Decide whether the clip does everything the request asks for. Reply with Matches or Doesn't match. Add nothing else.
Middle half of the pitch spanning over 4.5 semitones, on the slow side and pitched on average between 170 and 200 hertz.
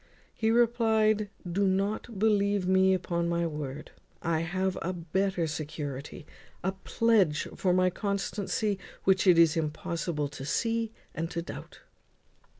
Doesn't match